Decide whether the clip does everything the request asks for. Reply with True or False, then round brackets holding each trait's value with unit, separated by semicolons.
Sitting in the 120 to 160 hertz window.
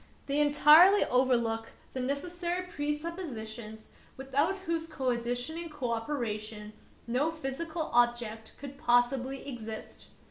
False (265 Hz)